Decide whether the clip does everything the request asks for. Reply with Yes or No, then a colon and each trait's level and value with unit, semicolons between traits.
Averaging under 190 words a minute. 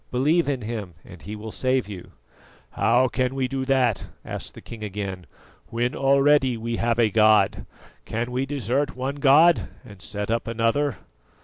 Yes: average, 170 wpm